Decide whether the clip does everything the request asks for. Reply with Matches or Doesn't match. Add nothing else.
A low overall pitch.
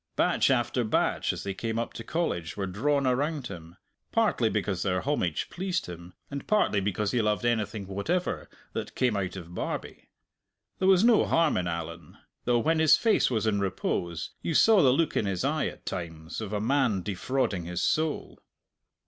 Matches